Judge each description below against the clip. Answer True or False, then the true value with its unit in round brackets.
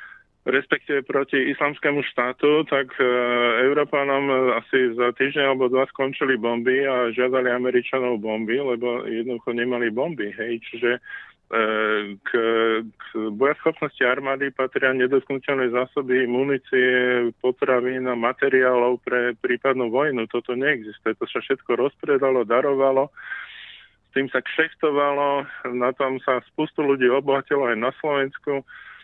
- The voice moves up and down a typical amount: False (2.0 semitones)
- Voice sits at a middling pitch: False (130 Hz)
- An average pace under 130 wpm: True (120 wpm)